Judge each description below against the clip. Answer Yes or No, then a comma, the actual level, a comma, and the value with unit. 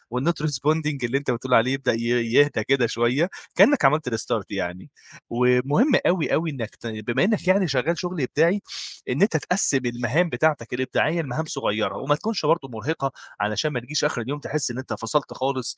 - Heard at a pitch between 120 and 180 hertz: Yes, low, 135 Hz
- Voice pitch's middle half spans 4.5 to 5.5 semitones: Yes, average, 4.8 semitones